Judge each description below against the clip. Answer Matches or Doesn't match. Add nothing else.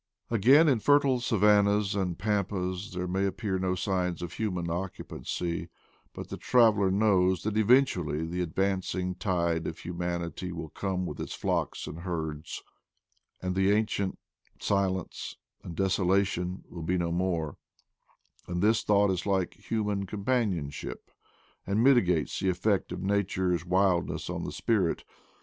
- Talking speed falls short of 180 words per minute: Matches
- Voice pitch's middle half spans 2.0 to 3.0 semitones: Matches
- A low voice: Matches